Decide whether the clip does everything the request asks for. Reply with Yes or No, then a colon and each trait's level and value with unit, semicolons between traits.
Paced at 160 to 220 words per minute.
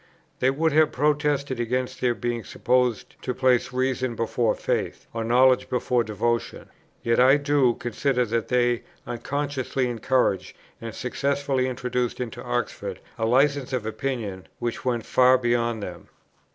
No: average, 140 wpm